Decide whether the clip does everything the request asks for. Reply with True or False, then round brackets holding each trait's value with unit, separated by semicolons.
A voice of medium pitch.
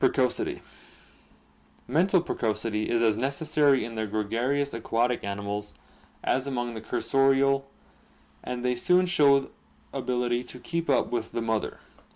False (125 Hz)